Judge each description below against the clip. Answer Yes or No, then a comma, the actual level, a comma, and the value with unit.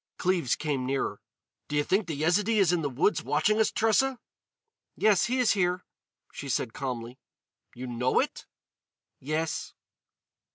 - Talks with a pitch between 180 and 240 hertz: No, medium, 160 Hz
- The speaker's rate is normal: Yes, average, 150 wpm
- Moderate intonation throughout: No, wide, 7.3 semitones